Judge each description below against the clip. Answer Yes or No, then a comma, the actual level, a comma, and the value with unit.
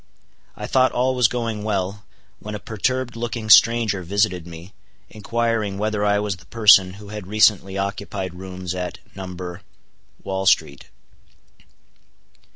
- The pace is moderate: No, slow, 130 wpm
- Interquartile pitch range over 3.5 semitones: No, average, 2.9 semitones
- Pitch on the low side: Yes, low, 100 Hz